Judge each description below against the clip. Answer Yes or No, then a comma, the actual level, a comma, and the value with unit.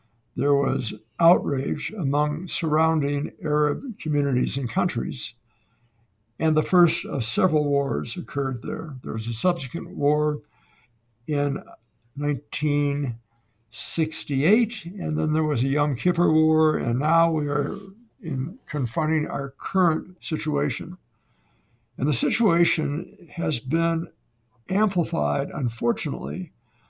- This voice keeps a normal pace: No, slow, 105 wpm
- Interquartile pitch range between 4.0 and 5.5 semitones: No, average, 3.6 semitones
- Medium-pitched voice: Yes, medium, 150 Hz